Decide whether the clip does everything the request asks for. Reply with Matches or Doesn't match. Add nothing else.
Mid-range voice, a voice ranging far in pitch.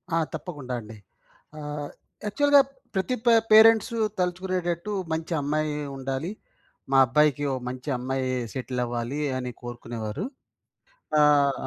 Matches